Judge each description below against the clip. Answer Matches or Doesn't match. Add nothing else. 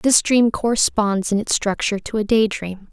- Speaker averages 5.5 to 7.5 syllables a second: Doesn't match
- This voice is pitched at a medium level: Doesn't match